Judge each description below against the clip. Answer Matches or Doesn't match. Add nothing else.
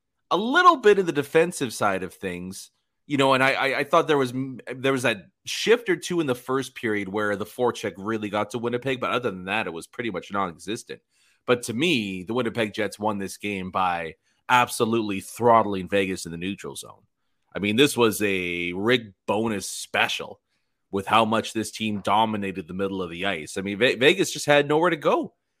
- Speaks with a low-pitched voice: Matches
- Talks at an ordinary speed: Doesn't match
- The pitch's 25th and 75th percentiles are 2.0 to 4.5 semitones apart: Doesn't match